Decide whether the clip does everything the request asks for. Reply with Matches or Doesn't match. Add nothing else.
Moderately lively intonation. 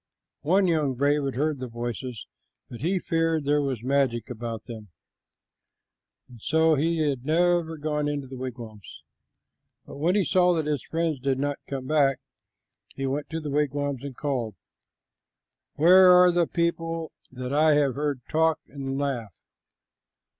Matches